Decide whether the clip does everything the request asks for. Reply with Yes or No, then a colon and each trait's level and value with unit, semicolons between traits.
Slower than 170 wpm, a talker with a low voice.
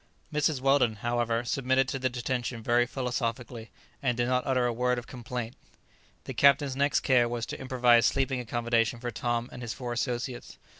No: average, 180 wpm; low, 125 Hz